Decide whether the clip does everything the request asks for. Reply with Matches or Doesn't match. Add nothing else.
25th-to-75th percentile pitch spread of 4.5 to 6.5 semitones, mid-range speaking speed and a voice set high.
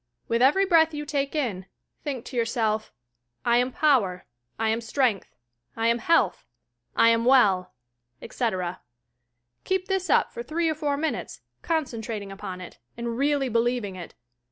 Matches